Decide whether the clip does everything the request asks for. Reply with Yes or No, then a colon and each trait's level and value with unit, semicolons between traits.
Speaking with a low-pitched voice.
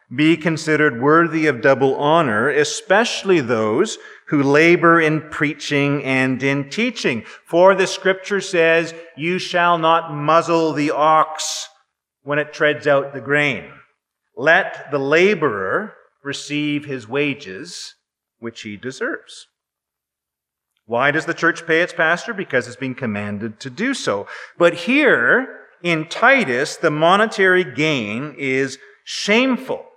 No: medium, 155 Hz